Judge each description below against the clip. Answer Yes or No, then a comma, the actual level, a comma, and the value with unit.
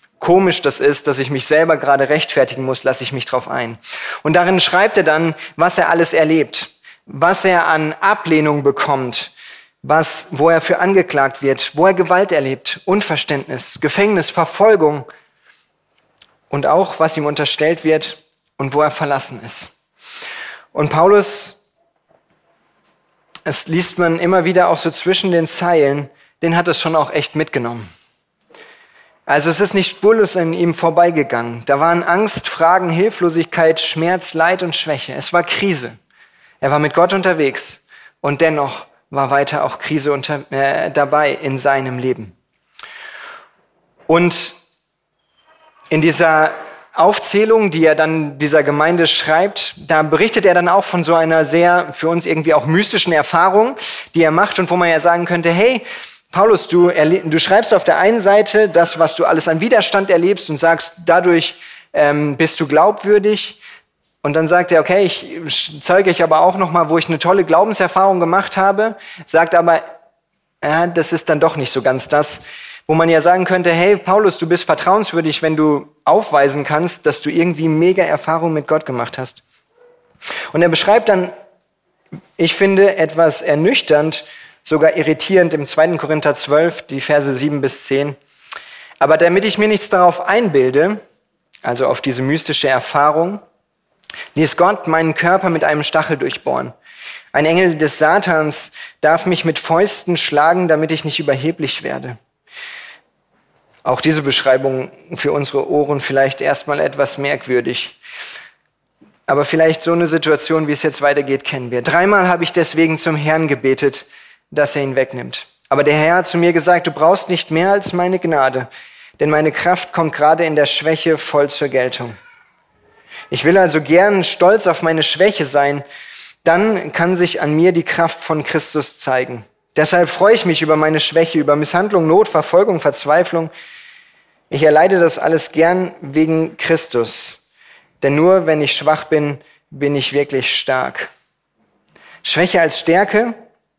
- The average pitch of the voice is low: No, medium, 160 Hz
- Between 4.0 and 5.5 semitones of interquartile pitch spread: No, average, 3.1 semitones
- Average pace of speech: Yes, average, 160 wpm